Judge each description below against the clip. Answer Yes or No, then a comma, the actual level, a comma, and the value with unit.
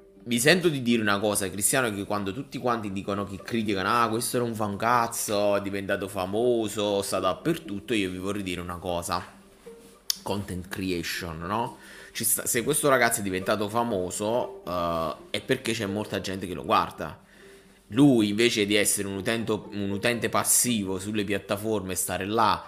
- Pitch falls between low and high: No, low, 105 Hz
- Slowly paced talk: No, average, 165 wpm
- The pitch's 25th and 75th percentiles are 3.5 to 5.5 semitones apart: No, average, 2.8 semitones